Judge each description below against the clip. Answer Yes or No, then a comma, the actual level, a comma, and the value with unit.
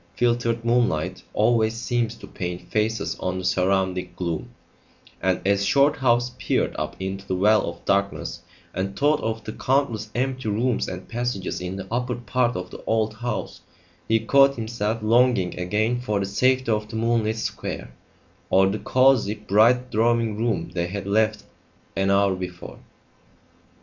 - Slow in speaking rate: No, average, 155 wpm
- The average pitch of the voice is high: No, low, 110 Hz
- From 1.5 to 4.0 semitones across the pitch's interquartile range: Yes, average, 3.6 semitones